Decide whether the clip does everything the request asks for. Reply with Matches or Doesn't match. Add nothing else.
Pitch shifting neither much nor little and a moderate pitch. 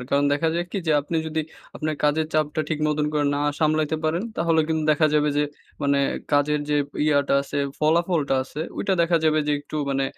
Doesn't match